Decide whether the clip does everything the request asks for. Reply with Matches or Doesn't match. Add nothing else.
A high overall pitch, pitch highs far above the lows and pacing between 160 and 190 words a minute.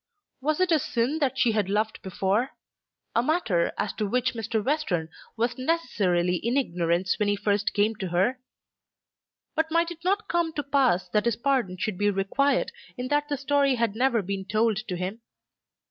Matches